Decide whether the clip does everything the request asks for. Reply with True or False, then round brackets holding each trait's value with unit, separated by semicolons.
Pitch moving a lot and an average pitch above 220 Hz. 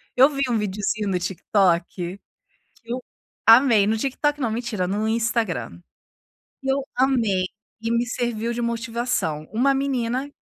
False (3.7 semitones; 230 Hz)